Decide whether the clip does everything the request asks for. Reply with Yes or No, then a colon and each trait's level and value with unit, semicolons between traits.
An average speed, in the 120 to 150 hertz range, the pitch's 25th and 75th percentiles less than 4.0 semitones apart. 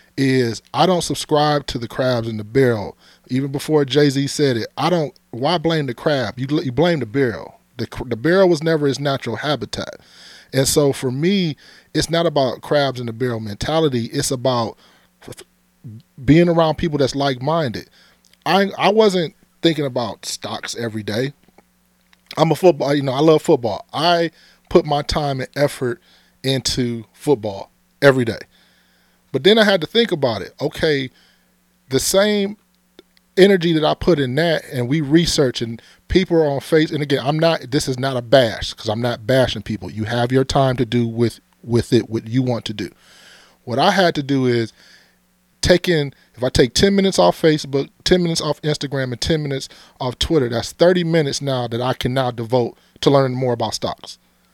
No: average, 190 wpm; low, 135 Hz; average, 5.1 semitones